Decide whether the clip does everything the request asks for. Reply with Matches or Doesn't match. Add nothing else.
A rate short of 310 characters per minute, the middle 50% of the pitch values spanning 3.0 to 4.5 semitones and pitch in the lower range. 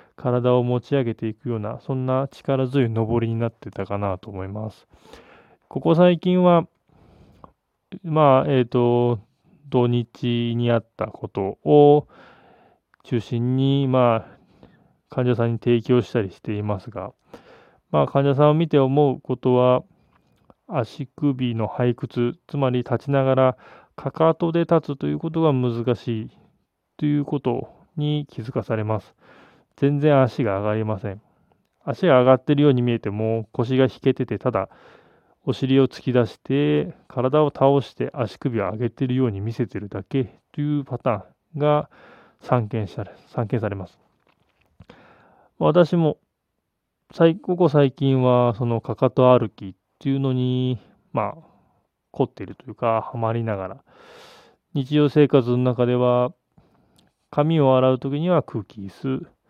Matches